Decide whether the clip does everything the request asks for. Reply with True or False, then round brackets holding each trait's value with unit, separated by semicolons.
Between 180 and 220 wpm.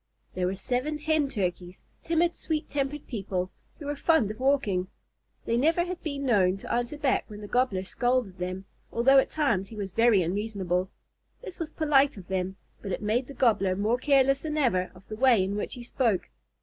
True (200 wpm)